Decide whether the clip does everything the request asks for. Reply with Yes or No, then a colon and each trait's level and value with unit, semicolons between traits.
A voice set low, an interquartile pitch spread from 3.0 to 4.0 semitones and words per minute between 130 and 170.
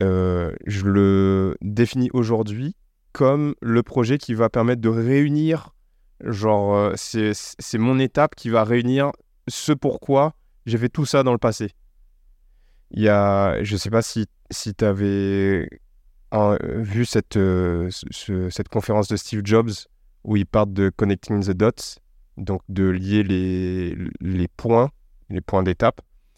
Yes: low, 105 Hz; average, 3.7 semitones; average, 150 wpm